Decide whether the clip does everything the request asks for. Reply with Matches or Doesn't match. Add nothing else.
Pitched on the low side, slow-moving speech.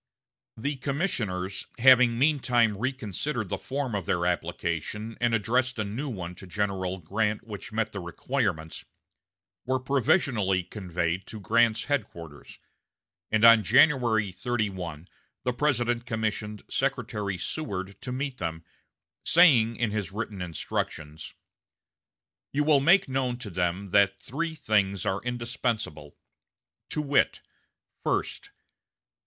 Matches